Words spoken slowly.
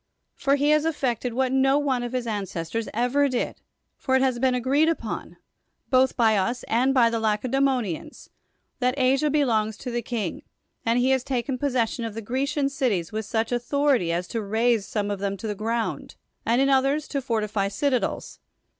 No: average, 185 wpm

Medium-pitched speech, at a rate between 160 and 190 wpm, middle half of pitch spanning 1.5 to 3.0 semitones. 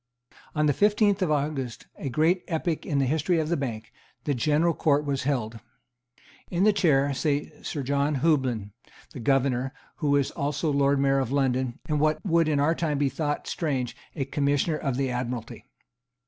Yes: medium, 145 Hz; average, 180 wpm; average, 2.7 semitones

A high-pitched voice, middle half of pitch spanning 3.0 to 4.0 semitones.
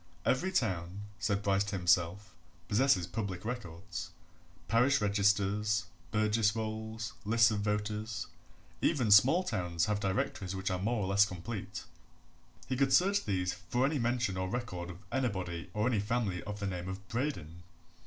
No: low, 105 Hz; average, 3.7 semitones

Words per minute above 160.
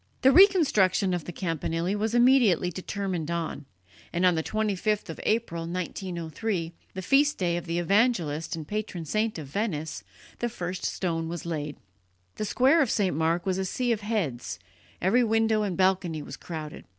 Yes: average, 170 wpm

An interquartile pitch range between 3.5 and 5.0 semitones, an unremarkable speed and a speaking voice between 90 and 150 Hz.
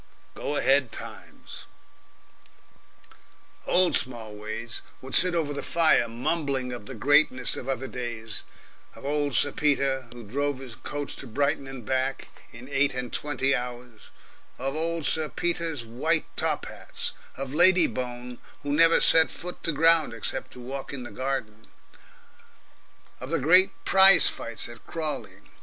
Yes: average, 3.9 semitones; average, 150 wpm; low, 135 Hz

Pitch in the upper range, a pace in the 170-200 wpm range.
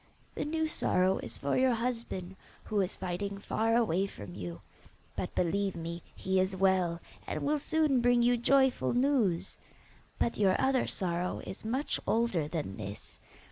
No: high, 200 Hz; average, 160 wpm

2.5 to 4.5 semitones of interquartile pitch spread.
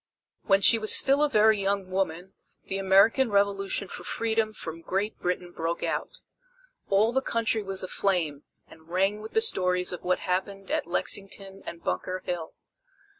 Yes: average, 2.8 semitones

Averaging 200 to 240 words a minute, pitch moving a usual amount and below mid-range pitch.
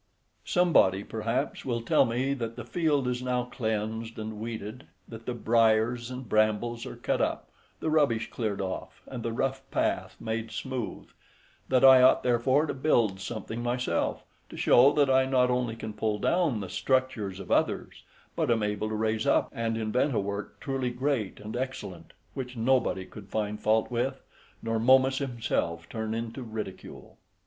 No: average, 170 wpm; average, 3.0 semitones; low, 115 Hz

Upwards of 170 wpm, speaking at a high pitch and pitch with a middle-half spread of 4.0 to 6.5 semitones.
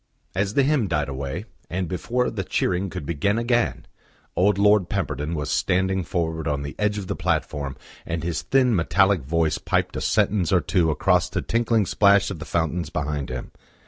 No: average, 185 wpm; very low, 90 Hz; average, 4.3 semitones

